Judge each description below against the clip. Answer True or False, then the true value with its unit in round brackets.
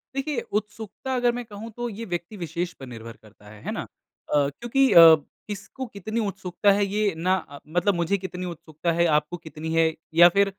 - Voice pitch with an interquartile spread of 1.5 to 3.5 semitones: False (4.6 semitones)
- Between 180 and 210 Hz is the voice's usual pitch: True (185 Hz)